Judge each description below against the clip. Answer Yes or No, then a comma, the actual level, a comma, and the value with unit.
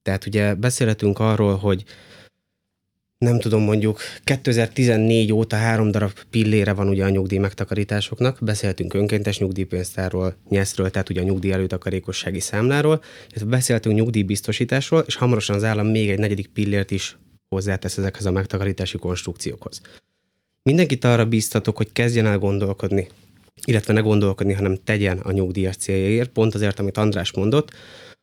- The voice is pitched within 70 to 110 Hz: Yes, low, 105 Hz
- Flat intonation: Yes, narrow, 2.3 semitones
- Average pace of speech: Yes, average, 140 wpm